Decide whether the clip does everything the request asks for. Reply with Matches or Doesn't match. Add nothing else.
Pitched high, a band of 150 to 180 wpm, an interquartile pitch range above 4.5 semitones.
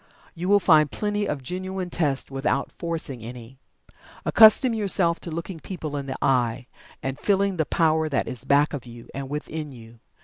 Doesn't match